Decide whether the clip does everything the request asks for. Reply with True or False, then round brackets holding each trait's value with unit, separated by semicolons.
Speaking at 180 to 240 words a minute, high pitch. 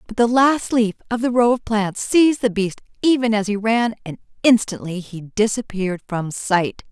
True (190 wpm; 215 Hz)